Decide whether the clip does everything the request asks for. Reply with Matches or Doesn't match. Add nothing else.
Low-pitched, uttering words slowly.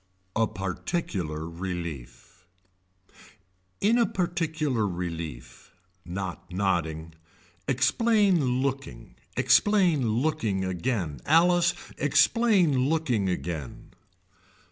Matches